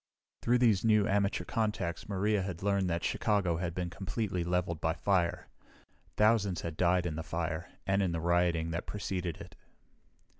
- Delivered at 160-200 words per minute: Yes, average, 165 wpm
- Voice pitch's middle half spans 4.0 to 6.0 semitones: No, average, 3.0 semitones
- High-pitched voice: No, very low, 90 Hz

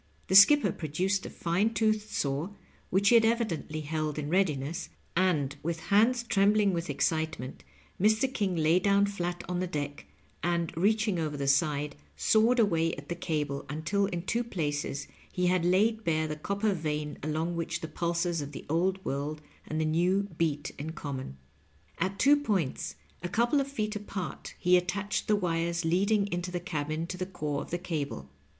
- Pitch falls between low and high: Yes, medium, 175 Hz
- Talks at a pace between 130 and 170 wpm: No, average, 185 wpm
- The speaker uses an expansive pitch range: No, average, 4.5 semitones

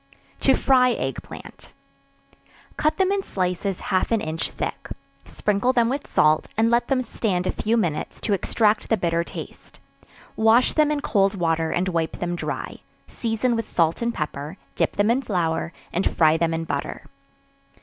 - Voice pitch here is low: No, high, 200 Hz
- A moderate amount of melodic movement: No, wide, 5.8 semitones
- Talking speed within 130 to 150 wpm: No, average, 170 wpm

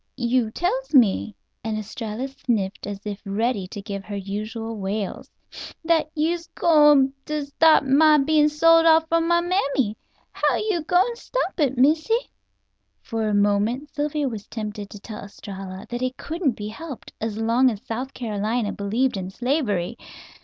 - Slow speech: No, average, 160 wpm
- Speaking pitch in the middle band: No, high, 245 Hz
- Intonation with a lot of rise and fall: Yes, wide, 6.6 semitones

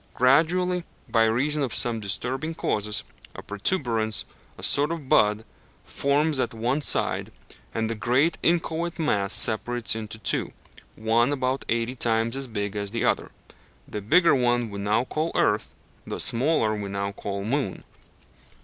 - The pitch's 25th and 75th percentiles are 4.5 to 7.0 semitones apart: Yes, average, 4.9 semitones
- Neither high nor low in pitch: No, low, 120 Hz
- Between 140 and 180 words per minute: Yes, average, 150 wpm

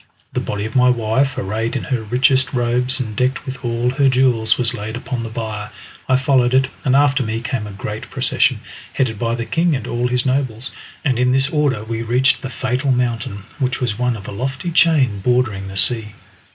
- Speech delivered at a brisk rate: Yes, fast, 210 wpm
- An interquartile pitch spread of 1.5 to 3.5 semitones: Yes, average, 2.8 semitones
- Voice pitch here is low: Yes, low, 125 Hz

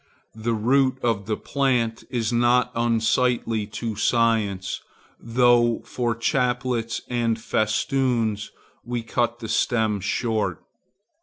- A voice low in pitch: Yes, low, 115 Hz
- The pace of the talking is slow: Yes, slow, 105 wpm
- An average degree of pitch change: No, narrow, 1.7 semitones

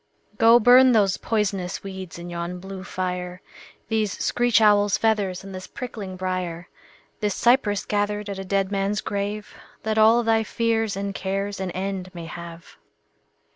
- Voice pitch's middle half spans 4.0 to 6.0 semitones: No, narrow, 2.6 semitones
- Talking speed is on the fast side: No, average, 155 wpm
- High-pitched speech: Yes, high, 200 Hz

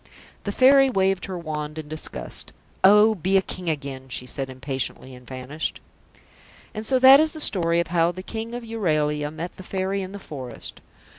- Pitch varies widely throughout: Yes, wide, 5.9 semitones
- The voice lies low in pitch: No, medium, 175 Hz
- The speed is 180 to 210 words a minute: Yes, average, 190 wpm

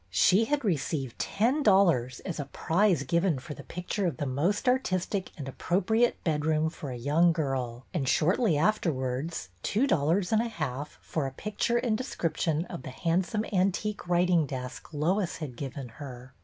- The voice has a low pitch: No, medium, 165 Hz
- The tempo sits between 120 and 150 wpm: No, average, 170 wpm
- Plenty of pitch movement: Yes, wide, 6.2 semitones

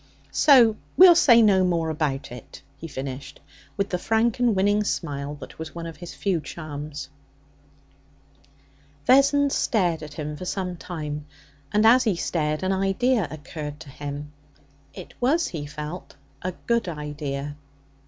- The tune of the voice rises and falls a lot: Yes, wide, 6.1 semitones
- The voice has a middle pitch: Yes, medium, 170 Hz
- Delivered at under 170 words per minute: Yes, average, 150 wpm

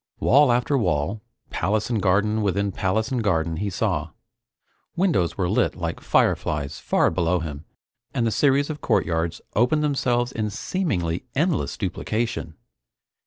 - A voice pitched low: Yes, low, 105 Hz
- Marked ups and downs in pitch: Yes, wide, 6.1 semitones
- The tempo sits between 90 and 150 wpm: Yes, average, 140 wpm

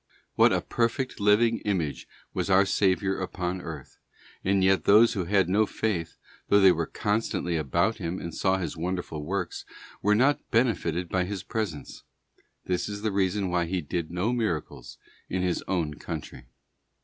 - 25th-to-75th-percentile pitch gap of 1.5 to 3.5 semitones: Yes, average, 3.1 semitones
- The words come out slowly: No, average, 165 wpm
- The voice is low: Yes, very low, 95 Hz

